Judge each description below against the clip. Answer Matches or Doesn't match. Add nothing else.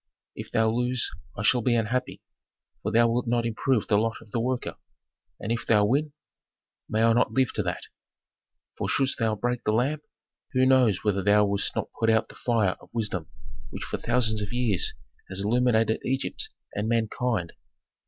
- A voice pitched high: Doesn't match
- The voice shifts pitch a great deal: Doesn't match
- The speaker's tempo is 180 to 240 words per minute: Matches